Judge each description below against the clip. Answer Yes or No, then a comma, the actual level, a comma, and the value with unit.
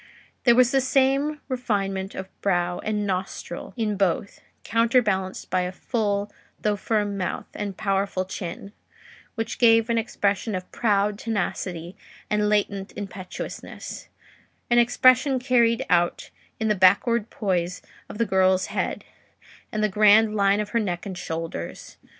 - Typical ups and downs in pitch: Yes, average, 3.3 semitones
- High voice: Yes, high, 205 Hz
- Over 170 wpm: No, average, 140 wpm